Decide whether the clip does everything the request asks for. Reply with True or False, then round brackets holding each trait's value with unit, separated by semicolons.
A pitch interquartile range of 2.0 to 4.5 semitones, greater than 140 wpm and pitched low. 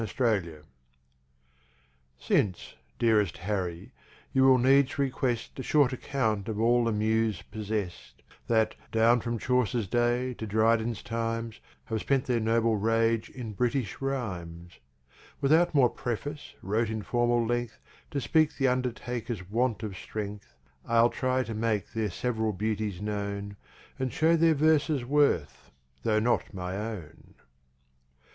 False (3.1 semitones; 135 wpm; 115 Hz)